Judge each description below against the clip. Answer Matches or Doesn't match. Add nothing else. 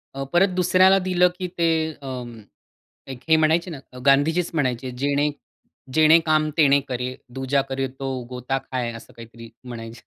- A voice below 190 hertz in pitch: Matches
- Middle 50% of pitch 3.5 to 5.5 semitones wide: Matches